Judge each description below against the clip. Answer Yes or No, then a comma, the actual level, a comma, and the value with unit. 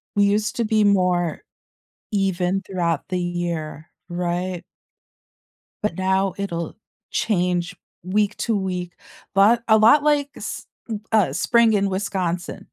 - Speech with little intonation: No, average, 3.0 semitones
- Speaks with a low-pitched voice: No, high, 190 Hz